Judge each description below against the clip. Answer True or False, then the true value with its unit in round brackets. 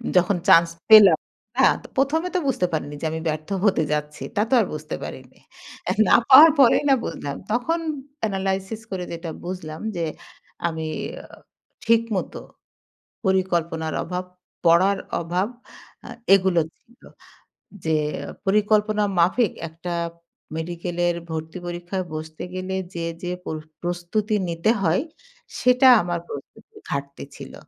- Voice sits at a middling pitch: True (180 Hz)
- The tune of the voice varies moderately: True (4.1 semitones)